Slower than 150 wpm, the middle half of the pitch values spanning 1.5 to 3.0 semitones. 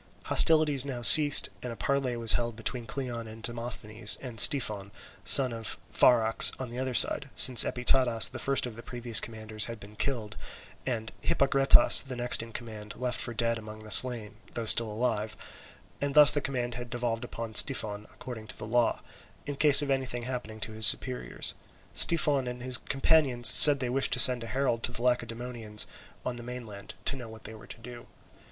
No: average, 190 wpm; narrow, 2.5 semitones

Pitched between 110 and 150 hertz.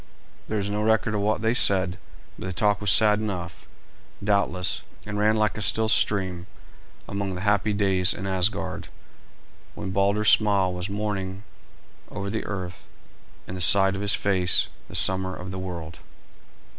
No: low, 100 Hz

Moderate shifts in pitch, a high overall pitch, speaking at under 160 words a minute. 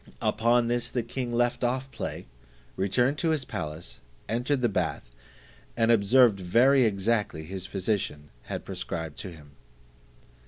No: average, 4.9 semitones; low, 115 Hz; slow, 135 wpm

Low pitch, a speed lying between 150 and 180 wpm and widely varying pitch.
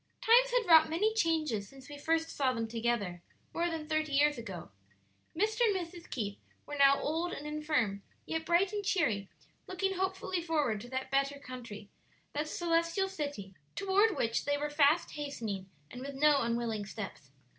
No: very high, 295 Hz; average, 170 wpm; wide, 6.2 semitones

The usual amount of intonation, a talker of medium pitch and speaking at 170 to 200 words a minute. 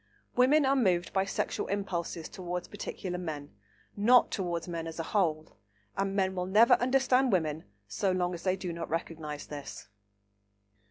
No: average, 3.5 semitones; medium, 180 Hz; average, 160 wpm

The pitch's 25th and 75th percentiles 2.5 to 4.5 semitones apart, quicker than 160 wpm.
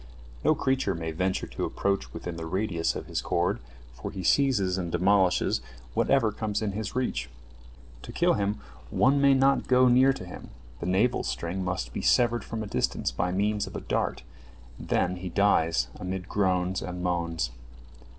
Yes: average, 3.7 semitones; average, 180 wpm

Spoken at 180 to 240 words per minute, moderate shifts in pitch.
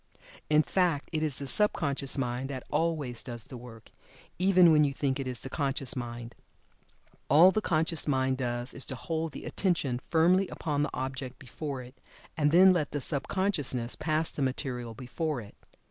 Yes: average, 185 wpm; average, 3.9 semitones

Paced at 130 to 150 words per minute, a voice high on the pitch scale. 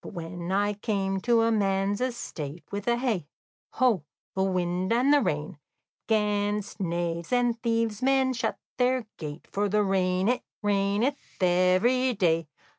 Yes: average, 140 wpm; high, 205 Hz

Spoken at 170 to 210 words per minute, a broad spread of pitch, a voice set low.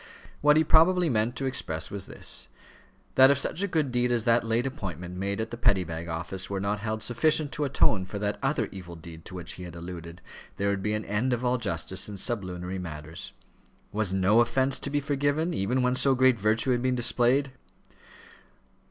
Yes: fast, 205 wpm; wide, 5.8 semitones; low, 110 Hz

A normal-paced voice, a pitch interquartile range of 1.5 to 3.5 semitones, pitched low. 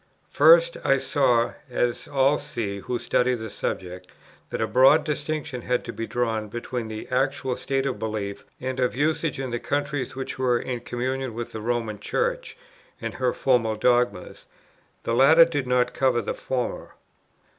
Yes: average, 165 wpm; average, 2.7 semitones; low, 125 Hz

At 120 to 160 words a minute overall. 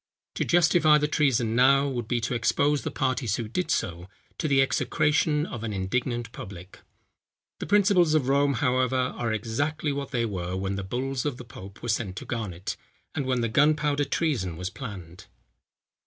No: average, 180 wpm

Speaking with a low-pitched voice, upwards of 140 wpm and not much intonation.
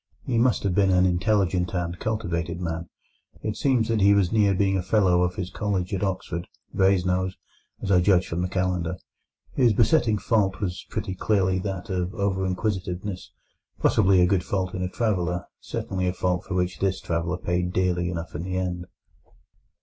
Yes: very low, 95 Hz; average, 180 wpm; narrow, 1.9 semitones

